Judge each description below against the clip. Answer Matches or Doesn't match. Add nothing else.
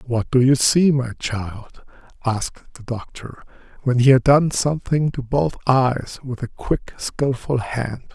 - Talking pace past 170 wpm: Doesn't match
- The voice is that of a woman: Doesn't match